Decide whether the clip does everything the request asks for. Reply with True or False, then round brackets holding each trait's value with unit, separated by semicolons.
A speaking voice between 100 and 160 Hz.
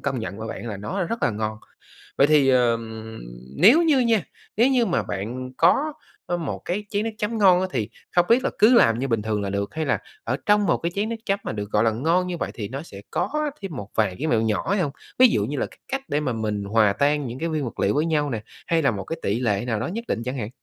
True (140 Hz)